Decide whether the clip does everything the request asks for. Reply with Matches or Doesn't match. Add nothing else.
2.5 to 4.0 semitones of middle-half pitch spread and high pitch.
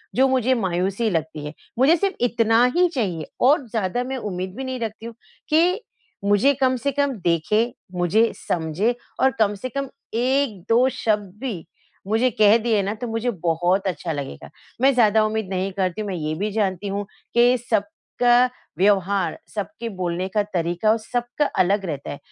Doesn't match